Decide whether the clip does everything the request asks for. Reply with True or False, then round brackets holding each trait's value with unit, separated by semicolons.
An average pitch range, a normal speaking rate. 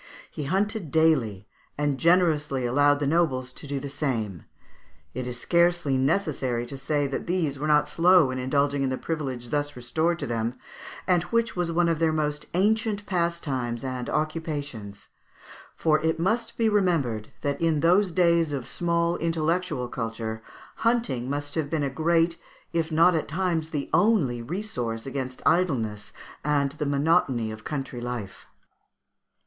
True (4.7 semitones; 155 wpm)